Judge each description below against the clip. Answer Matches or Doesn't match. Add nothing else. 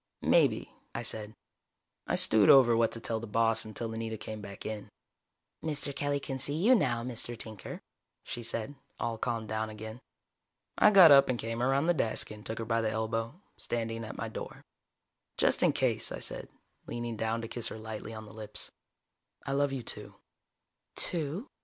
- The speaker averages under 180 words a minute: Doesn't match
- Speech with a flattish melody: Doesn't match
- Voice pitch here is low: Matches